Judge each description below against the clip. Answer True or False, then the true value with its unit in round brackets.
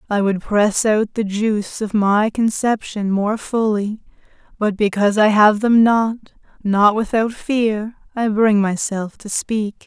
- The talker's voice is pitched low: False (210 Hz)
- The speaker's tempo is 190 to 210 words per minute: False (150 wpm)